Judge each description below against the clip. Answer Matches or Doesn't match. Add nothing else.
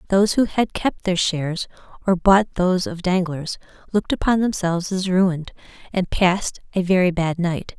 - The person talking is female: Matches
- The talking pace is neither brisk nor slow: Matches